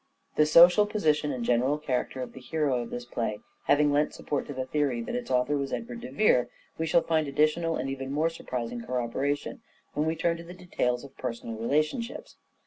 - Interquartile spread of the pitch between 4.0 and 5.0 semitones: Yes, average, 4.4 semitones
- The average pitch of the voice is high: No, medium, 145 Hz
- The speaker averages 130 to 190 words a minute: No, fast, 205 wpm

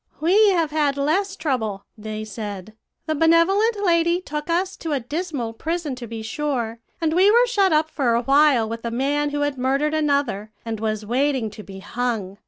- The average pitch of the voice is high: Yes, very high, 285 Hz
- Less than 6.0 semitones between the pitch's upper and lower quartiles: No, wide, 6.4 semitones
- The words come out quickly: No, average, 190 wpm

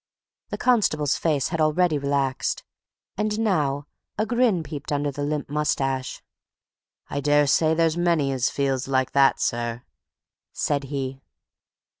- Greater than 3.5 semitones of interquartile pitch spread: No, average, 3.2 semitones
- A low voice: No, medium, 145 Hz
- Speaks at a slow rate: Yes, slow, 130 wpm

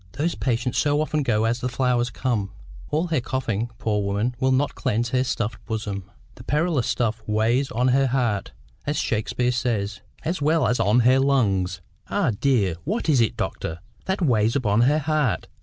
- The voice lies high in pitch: No, low, 125 Hz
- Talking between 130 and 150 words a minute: No, average, 180 wpm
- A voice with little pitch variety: No, average, 4.1 semitones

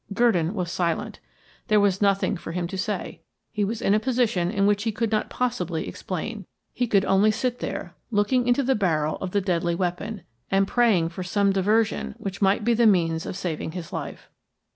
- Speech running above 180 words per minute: Yes, average, 200 wpm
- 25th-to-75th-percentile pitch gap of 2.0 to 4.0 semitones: Yes, average, 3.7 semitones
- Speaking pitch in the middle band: No, high, 195 Hz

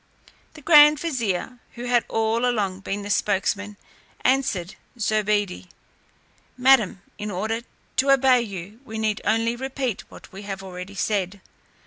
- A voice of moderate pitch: No, high, 215 Hz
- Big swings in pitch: No, average, 3.9 semitones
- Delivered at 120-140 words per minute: Yes, slow, 135 wpm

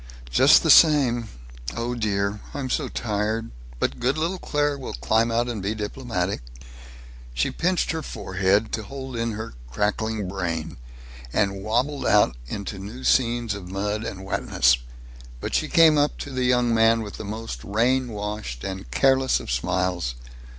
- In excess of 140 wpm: Yes, average, 160 wpm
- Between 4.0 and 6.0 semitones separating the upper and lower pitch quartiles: Yes, average, 4.3 semitones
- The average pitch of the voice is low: Yes, low, 110 Hz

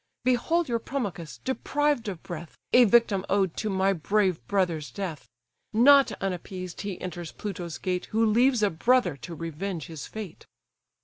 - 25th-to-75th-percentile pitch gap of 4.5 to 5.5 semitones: Yes, average, 5.2 semitones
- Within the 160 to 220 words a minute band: No, average, 150 wpm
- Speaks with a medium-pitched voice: No, high, 195 Hz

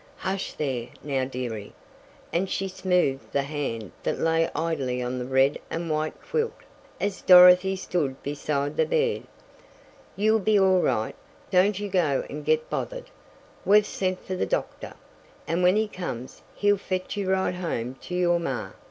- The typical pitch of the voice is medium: Yes, medium, 180 Hz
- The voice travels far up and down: Yes, wide, 5.8 semitones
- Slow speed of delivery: No, average, 160 wpm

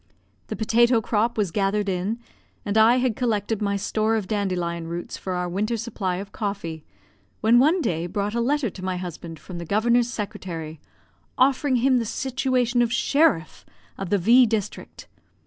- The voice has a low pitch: No, high, 210 Hz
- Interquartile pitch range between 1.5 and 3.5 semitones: No, average, 4.3 semitones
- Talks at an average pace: Yes, average, 170 wpm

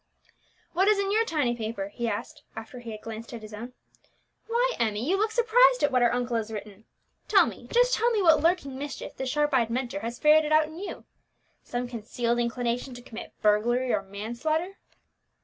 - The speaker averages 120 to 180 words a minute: No, average, 200 wpm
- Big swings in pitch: Yes, wide, 6.2 semitones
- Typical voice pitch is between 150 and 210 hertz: No, very high, 250 Hz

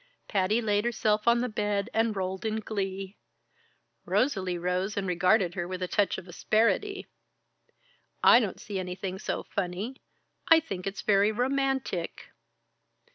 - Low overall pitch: No, high, 205 Hz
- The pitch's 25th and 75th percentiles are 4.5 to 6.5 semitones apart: No, average, 3.2 semitones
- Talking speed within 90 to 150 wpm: Yes, average, 140 wpm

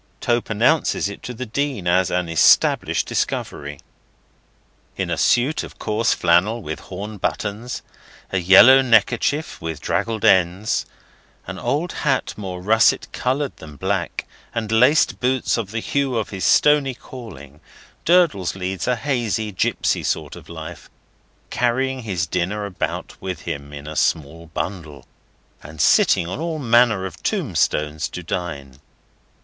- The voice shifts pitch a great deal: Yes, wide, 6.1 semitones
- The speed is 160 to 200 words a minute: No, average, 145 wpm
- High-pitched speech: No, low, 105 Hz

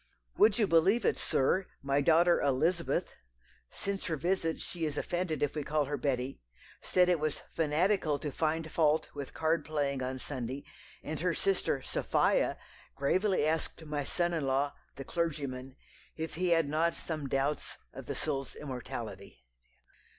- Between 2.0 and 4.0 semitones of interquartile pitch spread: Yes, average, 3.4 semitones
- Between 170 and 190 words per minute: No, average, 160 wpm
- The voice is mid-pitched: Yes, medium, 155 Hz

